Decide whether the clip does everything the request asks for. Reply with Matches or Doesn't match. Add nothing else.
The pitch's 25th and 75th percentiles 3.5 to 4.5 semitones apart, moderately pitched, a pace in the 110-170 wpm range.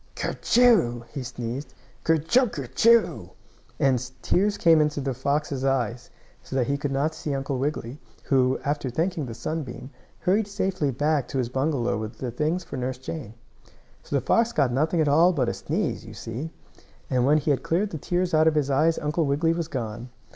Doesn't match